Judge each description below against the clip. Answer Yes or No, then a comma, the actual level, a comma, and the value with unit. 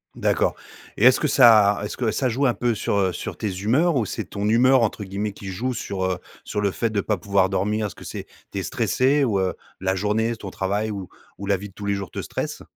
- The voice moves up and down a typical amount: Yes, average, 3.0 semitones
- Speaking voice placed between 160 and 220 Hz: No, low, 105 Hz